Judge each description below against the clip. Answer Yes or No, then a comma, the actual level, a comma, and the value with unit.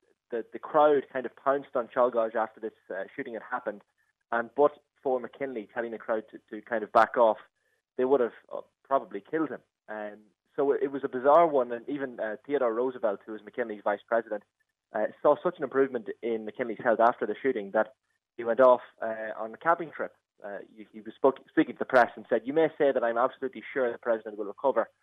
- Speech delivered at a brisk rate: Yes, fast, 220 wpm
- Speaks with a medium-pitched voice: No, low, 120 Hz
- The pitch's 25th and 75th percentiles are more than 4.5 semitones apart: No, average, 4.0 semitones